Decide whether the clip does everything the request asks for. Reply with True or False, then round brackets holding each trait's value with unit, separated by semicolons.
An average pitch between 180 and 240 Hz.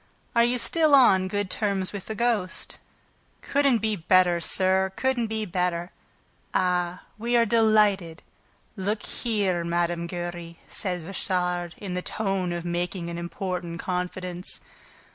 True (185 Hz)